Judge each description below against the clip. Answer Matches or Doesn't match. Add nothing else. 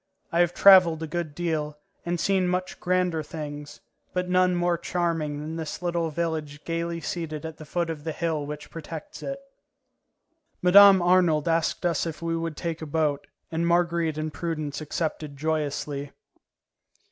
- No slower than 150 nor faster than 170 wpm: Matches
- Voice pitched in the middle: Matches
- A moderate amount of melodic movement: Doesn't match